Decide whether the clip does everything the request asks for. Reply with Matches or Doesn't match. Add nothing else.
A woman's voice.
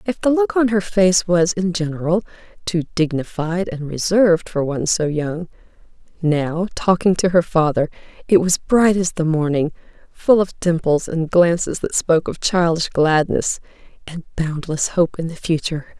Matches